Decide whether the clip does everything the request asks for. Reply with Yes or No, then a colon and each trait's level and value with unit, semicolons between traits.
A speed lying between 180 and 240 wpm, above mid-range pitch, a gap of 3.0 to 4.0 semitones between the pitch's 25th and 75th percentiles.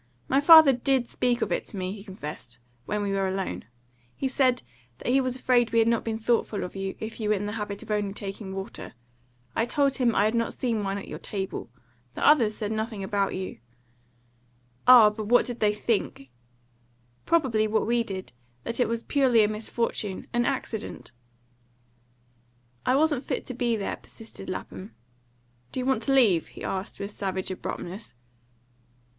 Yes: average, 185 wpm; high, 220 Hz; average, 3.7 semitones